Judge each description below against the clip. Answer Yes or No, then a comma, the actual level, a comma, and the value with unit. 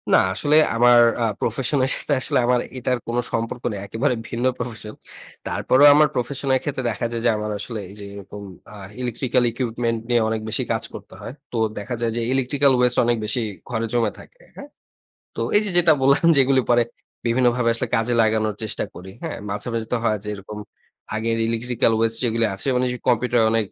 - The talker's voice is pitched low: Yes, low, 120 Hz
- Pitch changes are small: Yes, narrow, 2.1 semitones